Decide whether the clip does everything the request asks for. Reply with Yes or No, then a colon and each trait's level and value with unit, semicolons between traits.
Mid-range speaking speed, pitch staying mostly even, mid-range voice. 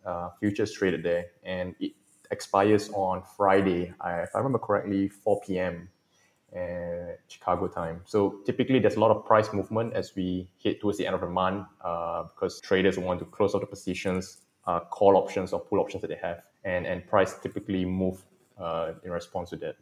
No: average, 190 wpm; narrow, 1.7 semitones; very low, 95 Hz